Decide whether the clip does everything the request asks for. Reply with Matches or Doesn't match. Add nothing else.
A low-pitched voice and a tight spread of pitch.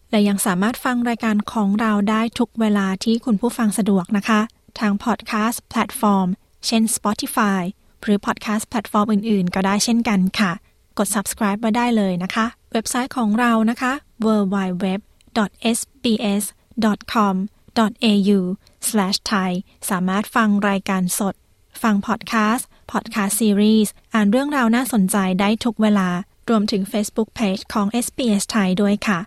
Doesn't match